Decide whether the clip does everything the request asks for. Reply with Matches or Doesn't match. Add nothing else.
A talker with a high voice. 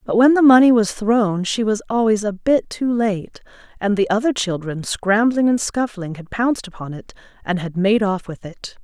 Matches